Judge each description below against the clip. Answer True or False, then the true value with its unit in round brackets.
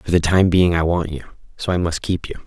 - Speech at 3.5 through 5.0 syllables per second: False (5.5 syllables/s)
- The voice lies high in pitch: False (85 Hz)